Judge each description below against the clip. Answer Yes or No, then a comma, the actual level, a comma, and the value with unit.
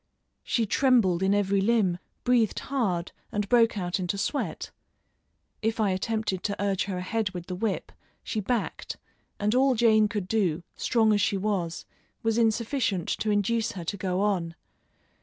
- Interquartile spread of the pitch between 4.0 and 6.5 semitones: No, average, 3.3 semitones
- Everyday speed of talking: Yes, average, 160 wpm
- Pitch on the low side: No, high, 205 Hz